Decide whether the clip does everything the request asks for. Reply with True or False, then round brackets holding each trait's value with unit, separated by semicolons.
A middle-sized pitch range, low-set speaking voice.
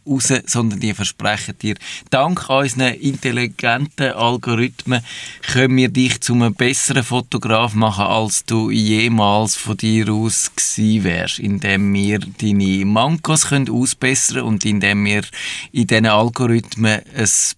True (3.3 semitones; 115 Hz)